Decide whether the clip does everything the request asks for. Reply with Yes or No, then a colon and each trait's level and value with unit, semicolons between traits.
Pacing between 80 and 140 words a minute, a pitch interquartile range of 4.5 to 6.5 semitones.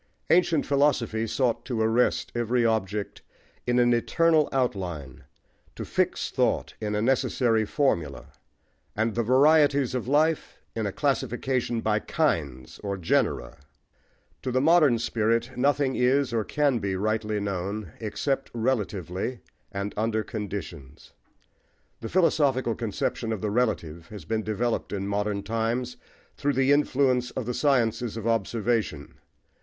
No: slow, 135 wpm; average, 3.8 semitones